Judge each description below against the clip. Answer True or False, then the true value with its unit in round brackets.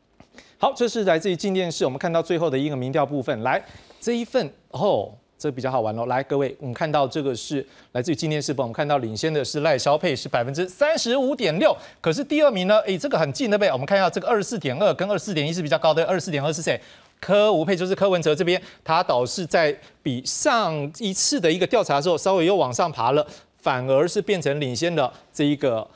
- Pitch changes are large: True (6.1 semitones)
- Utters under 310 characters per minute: False (365 characters per minute)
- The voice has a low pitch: False (160 Hz)